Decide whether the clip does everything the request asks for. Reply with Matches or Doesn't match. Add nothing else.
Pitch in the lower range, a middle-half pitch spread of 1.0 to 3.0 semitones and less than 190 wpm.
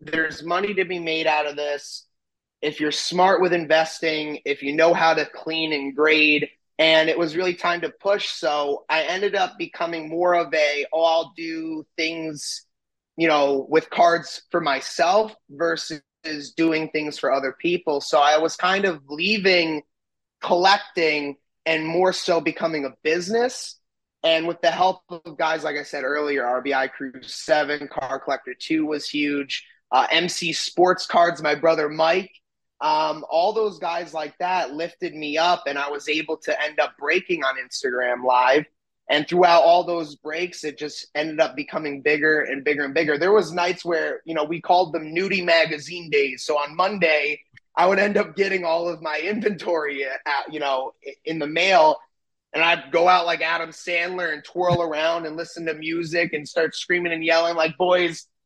Doesn't match